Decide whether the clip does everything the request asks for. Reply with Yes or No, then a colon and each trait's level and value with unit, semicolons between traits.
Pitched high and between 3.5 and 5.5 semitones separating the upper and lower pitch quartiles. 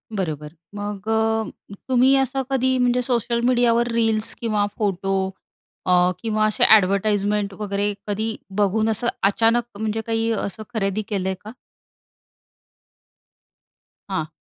No: high, 215 Hz; average, 2.9 semitones